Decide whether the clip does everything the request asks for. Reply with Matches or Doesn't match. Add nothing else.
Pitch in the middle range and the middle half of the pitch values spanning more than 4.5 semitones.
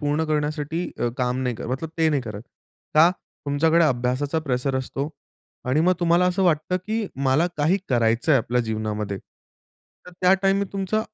Matches